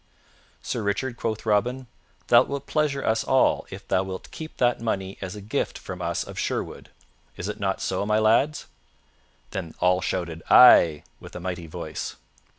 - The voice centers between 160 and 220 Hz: No, low, 105 Hz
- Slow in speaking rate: No, average, 170 wpm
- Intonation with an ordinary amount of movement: Yes, average, 4.8 semitones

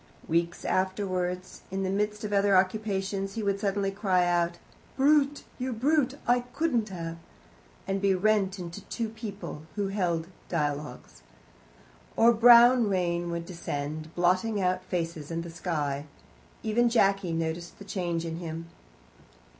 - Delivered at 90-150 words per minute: Yes, average, 145 wpm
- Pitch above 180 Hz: Yes, high, 190 Hz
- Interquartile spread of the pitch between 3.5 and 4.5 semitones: Yes, average, 3.8 semitones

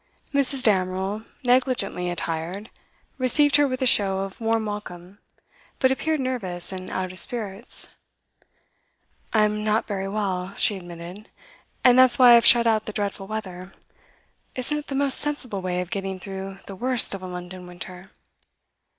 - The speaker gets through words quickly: No, average, 160 wpm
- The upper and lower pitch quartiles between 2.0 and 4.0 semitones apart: No, average, 4.9 semitones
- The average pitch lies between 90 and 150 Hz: No, high, 205 Hz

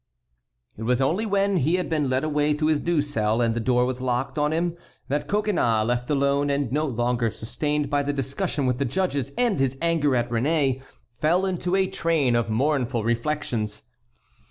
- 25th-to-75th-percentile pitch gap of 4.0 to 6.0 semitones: Yes, average, 4.5 semitones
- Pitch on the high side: No, medium, 140 Hz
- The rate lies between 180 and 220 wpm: Yes, average, 190 wpm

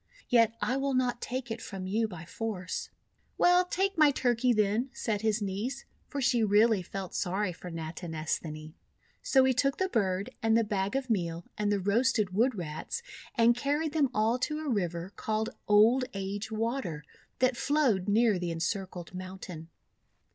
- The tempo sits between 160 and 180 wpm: Yes, average, 170 wpm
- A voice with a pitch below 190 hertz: No, high, 215 Hz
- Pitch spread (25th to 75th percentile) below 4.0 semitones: No, average, 5.3 semitones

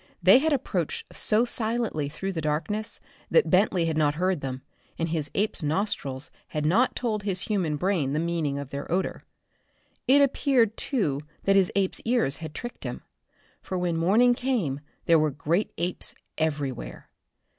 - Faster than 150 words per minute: Yes, average, 165 wpm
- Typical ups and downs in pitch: No, wide, 6.2 semitones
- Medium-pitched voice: Yes, medium, 180 Hz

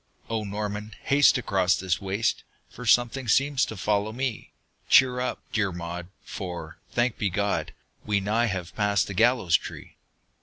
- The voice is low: Yes, low, 105 Hz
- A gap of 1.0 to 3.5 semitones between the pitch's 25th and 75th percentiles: No, average, 3.9 semitones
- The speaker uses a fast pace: No, average, 155 wpm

